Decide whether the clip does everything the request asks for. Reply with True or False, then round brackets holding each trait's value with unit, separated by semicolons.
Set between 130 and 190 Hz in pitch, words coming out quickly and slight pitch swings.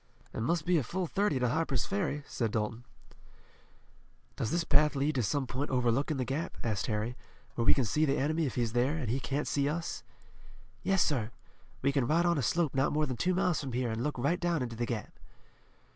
False (140 Hz; 220 wpm; 4.6 semitones)